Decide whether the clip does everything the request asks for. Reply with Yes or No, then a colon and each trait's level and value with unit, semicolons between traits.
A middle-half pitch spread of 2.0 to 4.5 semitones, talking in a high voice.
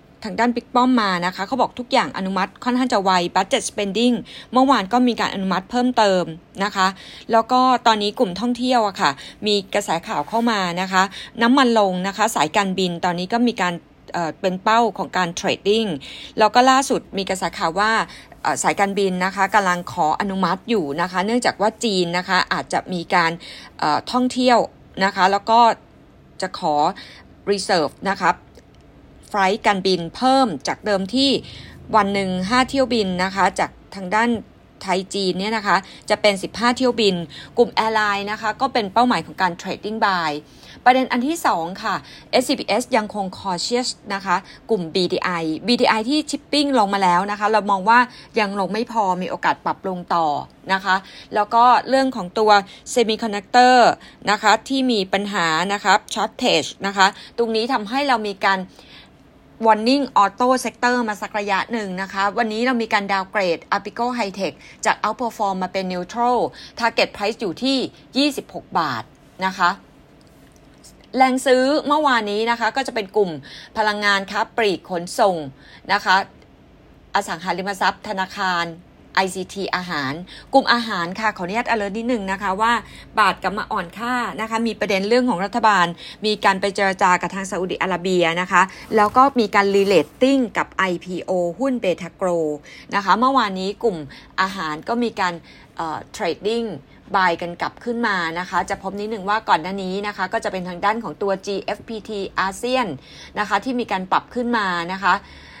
Yes: average, 4.0 semitones; high, 205 Hz